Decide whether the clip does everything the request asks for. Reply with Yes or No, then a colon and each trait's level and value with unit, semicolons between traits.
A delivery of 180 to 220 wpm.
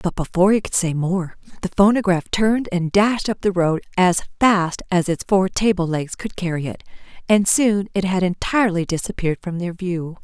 Yes: average, 195 wpm